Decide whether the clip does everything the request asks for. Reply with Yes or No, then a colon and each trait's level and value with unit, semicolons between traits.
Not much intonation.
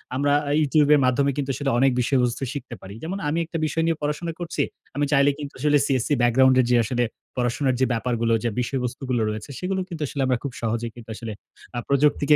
No: average, 3.3 semitones